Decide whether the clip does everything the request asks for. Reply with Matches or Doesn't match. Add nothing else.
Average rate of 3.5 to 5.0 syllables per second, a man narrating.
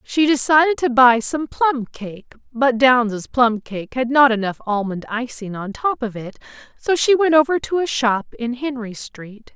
Doesn't match